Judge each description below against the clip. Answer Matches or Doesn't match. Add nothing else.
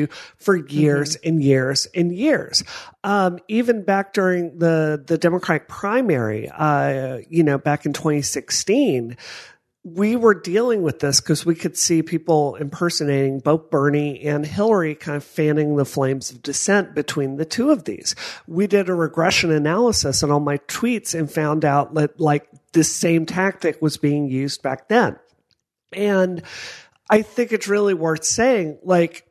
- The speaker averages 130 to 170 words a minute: Matches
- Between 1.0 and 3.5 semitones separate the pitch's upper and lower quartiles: Doesn't match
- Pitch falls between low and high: Matches